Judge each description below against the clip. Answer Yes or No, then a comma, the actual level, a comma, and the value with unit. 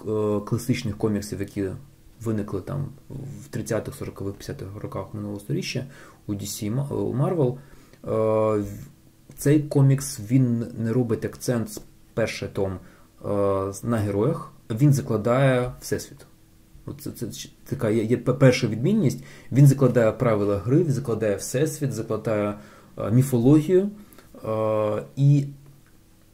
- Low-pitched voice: Yes, low, 115 Hz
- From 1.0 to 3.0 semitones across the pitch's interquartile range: No, average, 4.2 semitones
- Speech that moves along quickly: No, slow, 105 wpm